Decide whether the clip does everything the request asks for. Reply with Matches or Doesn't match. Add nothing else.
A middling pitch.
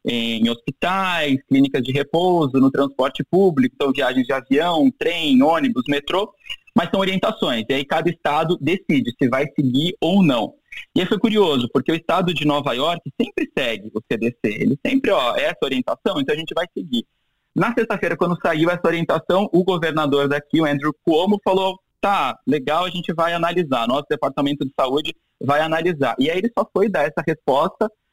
Matches